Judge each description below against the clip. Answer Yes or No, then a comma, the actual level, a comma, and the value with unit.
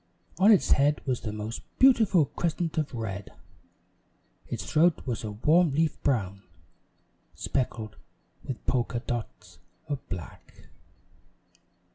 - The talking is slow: Yes, slow, 115 wpm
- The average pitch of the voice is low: Yes, low, 130 Hz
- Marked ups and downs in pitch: Yes, wide, 6.6 semitones